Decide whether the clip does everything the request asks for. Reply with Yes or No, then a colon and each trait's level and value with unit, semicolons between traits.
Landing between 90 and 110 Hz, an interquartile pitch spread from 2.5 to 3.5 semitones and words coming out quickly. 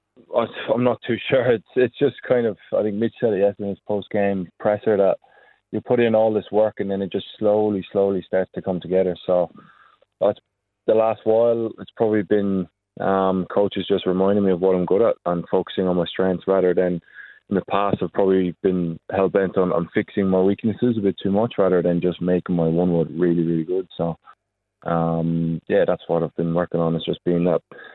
Yes: very low, 95 Hz; average, 2.9 semitones; fast, 215 wpm